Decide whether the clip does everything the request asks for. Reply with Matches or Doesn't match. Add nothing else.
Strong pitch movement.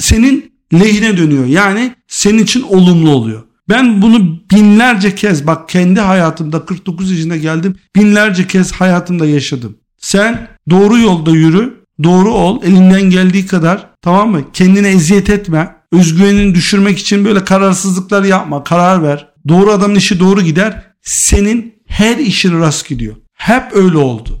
Doesn't match